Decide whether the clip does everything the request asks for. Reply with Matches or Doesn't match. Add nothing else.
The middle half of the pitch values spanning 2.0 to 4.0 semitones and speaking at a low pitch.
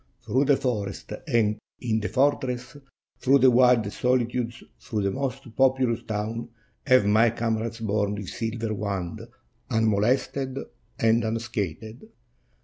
Matches